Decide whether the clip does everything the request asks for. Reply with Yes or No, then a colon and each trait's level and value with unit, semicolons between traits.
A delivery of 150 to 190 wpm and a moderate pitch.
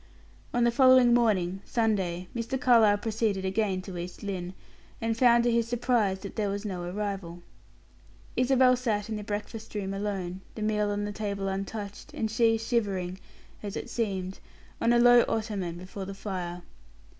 No: average, 165 wpm; high, 205 Hz